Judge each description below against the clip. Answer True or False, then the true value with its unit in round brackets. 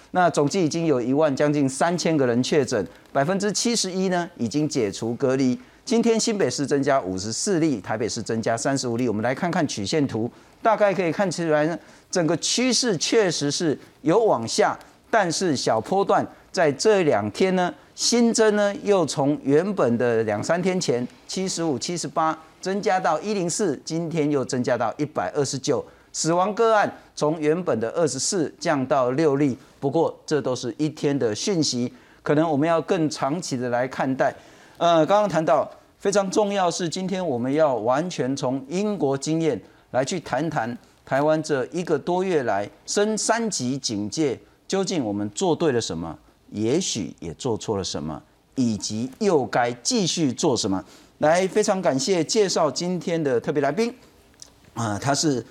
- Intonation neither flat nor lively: False (5.8 semitones)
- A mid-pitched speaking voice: True (155 Hz)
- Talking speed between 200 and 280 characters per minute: True (255 characters per minute)